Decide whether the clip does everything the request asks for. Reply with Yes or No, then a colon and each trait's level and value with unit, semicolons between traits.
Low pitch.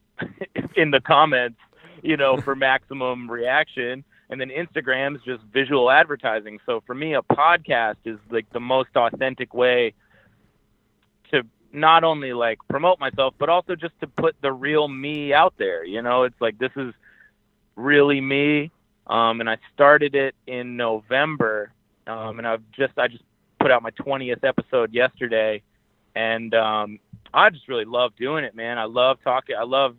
Yes: low, 125 Hz